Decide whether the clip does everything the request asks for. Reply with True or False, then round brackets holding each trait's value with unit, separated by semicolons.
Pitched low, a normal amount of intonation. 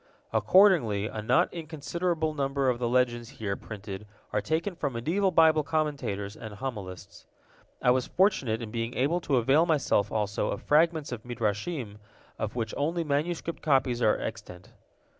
False (130 Hz; 6.5 semitones)